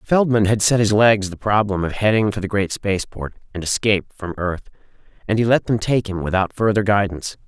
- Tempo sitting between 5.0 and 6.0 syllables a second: Yes, 5.8 syllables/s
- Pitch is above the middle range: No, low, 105 Hz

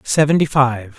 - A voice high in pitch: No, low, 135 Hz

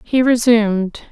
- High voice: Yes, high, 230 Hz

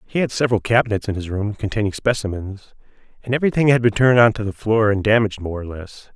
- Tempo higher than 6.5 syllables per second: Yes, 6.7 syllables/s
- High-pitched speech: No, low, 110 Hz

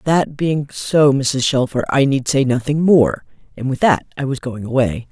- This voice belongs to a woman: Yes, female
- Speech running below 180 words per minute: No, average, 200 wpm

